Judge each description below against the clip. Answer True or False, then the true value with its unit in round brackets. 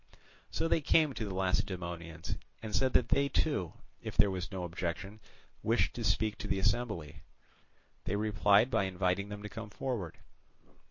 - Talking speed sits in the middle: True (165 wpm)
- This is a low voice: True (100 Hz)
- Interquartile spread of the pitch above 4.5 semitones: False (3.3 semitones)